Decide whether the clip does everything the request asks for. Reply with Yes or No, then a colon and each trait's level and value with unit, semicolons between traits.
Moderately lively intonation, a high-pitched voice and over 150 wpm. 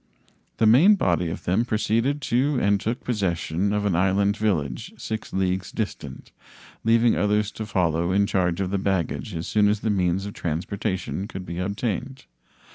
No: average, 3.2 semitones; low, 100 Hz; average, 170 wpm